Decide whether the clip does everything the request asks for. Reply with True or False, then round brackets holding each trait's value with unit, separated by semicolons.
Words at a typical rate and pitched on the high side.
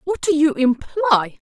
True (160 wpm; 285 Hz)